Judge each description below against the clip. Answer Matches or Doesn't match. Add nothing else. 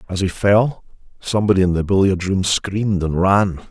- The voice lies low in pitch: Matches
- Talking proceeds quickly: Doesn't match